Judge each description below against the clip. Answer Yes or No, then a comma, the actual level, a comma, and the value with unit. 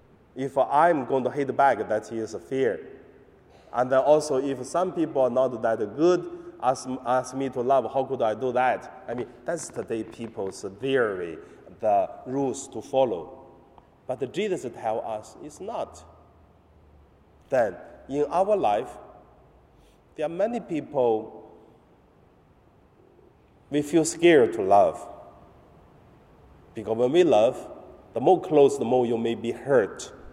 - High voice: No, low, 130 Hz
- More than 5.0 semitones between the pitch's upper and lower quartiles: No, average, 4.5 semitones